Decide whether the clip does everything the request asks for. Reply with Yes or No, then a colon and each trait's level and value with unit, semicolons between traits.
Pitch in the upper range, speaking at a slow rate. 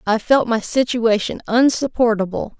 Yes: high, 230 Hz; slow, 115 wpm